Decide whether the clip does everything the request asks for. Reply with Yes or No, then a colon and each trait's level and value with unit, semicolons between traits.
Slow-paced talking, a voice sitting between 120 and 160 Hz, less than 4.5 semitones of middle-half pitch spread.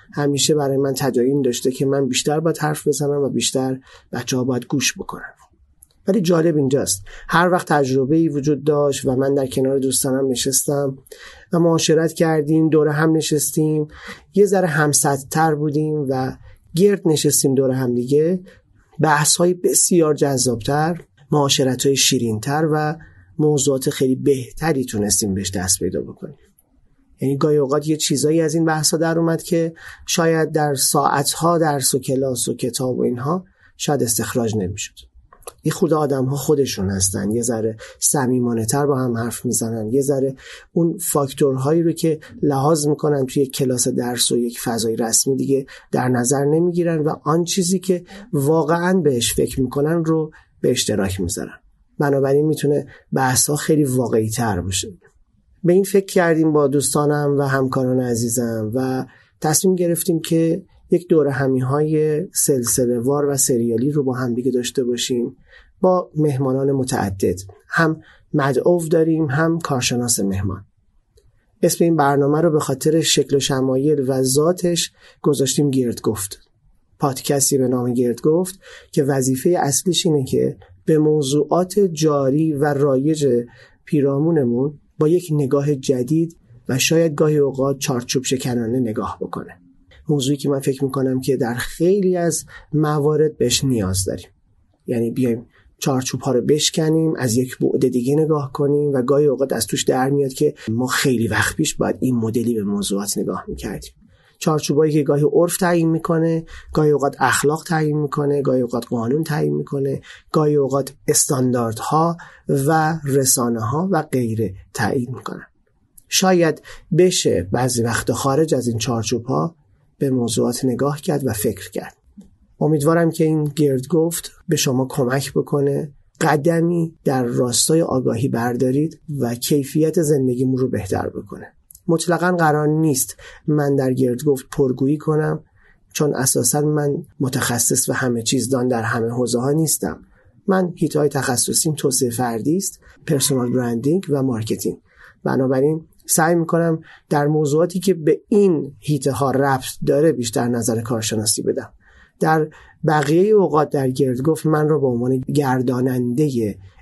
No: average, 145 wpm; medium, 140 Hz; average, 3.7 semitones